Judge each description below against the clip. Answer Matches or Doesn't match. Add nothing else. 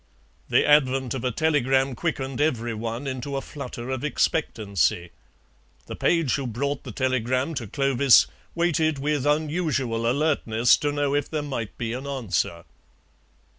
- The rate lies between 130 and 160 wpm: Matches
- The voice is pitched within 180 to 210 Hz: Doesn't match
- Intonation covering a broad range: Doesn't match